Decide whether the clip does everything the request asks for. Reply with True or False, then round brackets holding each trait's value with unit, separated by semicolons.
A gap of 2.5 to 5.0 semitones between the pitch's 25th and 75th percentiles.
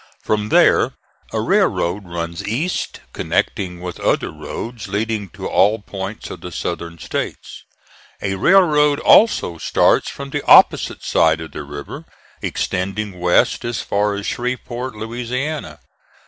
False (5.5 semitones)